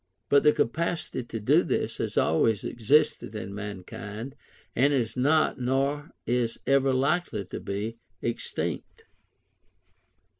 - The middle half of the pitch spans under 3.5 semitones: No, average, 4.6 semitones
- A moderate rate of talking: No, slow, 120 wpm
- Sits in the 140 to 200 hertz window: No, low, 125 Hz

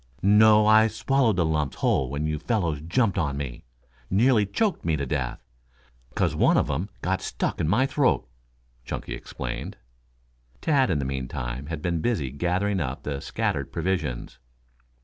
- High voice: No, very low, 85 Hz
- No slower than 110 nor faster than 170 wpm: Yes, average, 160 wpm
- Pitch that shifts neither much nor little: No, wide, 7.1 semitones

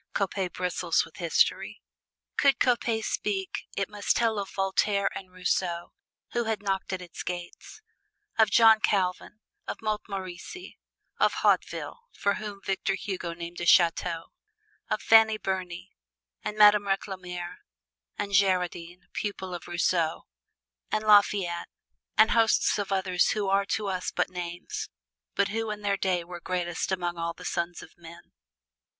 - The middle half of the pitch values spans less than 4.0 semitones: Yes, average, 2.8 semitones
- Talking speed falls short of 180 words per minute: Yes, average, 145 wpm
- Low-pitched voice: No, high, 190 Hz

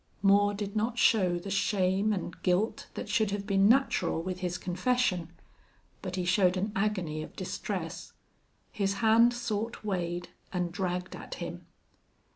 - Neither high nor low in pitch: No, high, 195 Hz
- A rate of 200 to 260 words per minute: No, average, 150 wpm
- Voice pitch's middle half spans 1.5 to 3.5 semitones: Yes, average, 2.9 semitones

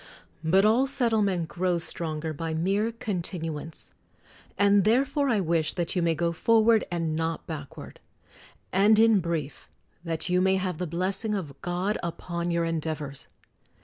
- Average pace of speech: Yes, average, 145 wpm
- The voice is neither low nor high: Yes, medium, 175 Hz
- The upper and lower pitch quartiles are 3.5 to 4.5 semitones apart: Yes, average, 4.0 semitones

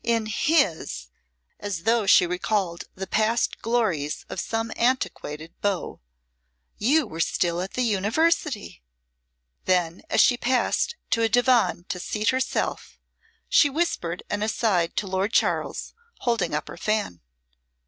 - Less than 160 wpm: Yes, average, 140 wpm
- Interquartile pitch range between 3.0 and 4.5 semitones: No, average, 5.2 semitones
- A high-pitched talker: Yes, high, 210 Hz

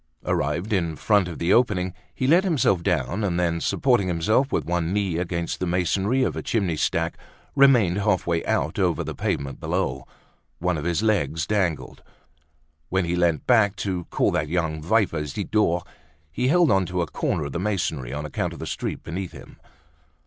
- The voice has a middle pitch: No, very low, 90 Hz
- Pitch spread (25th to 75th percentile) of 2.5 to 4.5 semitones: Yes, average, 3.9 semitones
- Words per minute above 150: Yes, average, 185 wpm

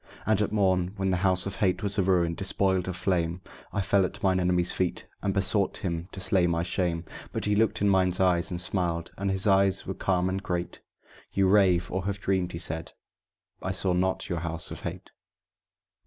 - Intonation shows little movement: Yes, narrow, 1.7 semitones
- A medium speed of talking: No, fast, 210 wpm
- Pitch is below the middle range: Yes, very low, 95 Hz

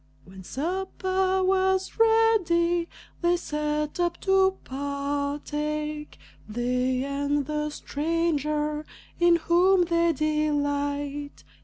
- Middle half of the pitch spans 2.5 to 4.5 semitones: Yes, average, 3.5 semitones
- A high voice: Yes, very high, 300 Hz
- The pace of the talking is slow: Yes, slow, 90 wpm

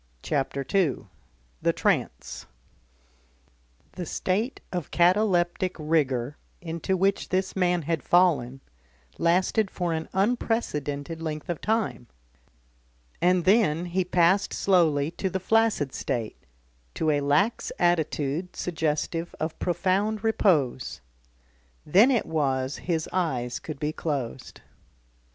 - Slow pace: Yes, slow, 110 wpm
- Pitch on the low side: No, medium, 170 Hz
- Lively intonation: No, average, 4.2 semitones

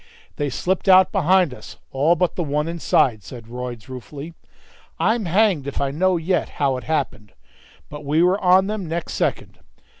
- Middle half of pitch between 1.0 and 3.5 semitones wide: No, average, 5.1 semitones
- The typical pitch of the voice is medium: Yes, medium, 160 Hz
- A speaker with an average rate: Yes, average, 175 wpm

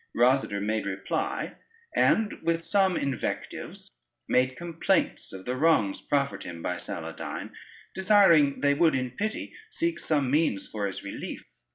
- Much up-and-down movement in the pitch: Yes, wide, 7.3 semitones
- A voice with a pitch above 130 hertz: Yes, medium, 140 Hz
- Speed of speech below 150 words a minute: Yes, average, 140 wpm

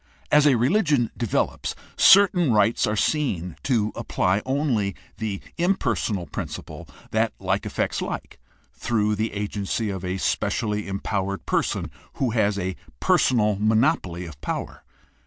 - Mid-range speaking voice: No, low, 105 Hz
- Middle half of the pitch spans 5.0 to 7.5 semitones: No, average, 4.6 semitones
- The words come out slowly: Yes, slow, 130 wpm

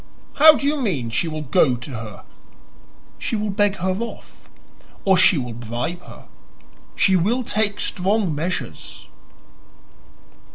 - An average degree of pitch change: No, wide, 7.4 semitones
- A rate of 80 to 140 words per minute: Yes, slow, 135 wpm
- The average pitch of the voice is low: No, medium, 185 Hz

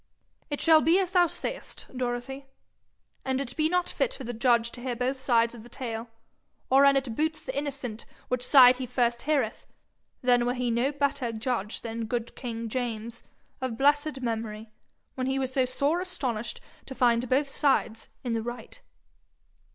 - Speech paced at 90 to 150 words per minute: No, average, 180 wpm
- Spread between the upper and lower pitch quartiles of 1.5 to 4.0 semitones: Yes, average, 2.9 semitones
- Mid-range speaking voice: No, very high, 250 Hz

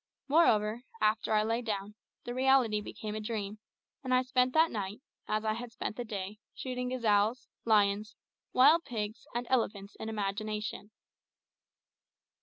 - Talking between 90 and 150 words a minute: Yes, average, 145 wpm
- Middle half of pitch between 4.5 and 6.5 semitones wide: No, average, 3.0 semitones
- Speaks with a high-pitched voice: Yes, high, 220 Hz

